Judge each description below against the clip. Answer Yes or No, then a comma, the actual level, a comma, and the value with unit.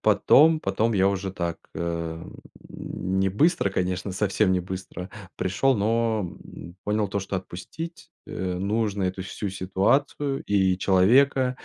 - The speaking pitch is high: No, low, 100 Hz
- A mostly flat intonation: No, average, 3.5 semitones